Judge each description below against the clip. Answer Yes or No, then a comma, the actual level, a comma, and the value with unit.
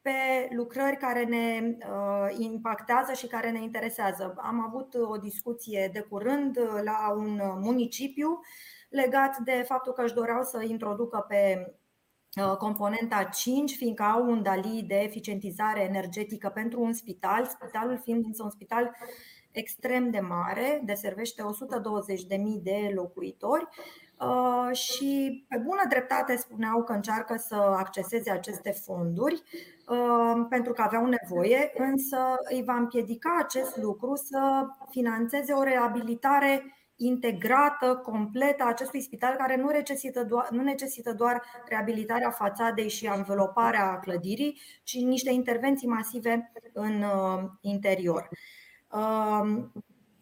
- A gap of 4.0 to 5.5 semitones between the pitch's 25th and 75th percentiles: No, average, 3.5 semitones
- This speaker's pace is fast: No, average, 125 wpm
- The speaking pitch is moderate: No, high, 235 Hz